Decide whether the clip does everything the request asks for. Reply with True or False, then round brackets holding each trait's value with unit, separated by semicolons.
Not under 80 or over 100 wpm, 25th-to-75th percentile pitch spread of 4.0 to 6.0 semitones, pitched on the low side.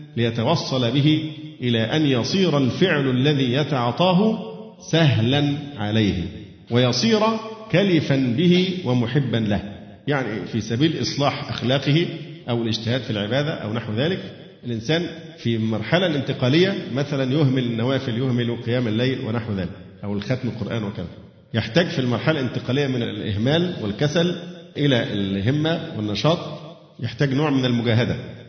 False (120 wpm; 5.4 semitones; 130 Hz)